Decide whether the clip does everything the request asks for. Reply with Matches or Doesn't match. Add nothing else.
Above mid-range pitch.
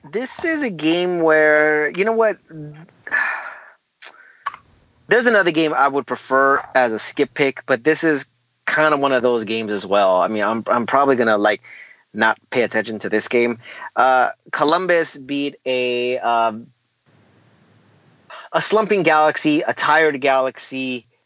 Doesn't match